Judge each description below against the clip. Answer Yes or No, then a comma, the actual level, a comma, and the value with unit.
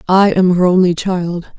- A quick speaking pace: No, average, 190 wpm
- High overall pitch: No, medium, 180 Hz